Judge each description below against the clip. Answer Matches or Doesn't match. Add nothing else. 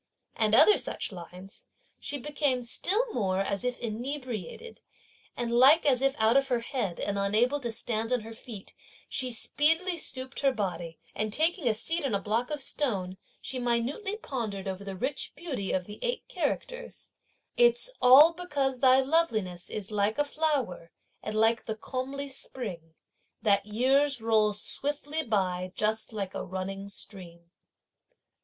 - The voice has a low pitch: Doesn't match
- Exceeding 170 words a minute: Doesn't match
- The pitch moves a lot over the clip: Matches